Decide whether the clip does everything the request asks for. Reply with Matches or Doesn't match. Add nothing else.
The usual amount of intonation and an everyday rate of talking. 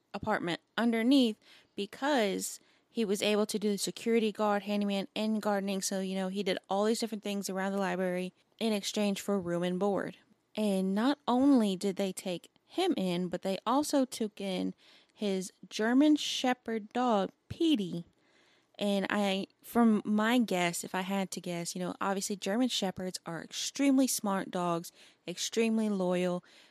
Matches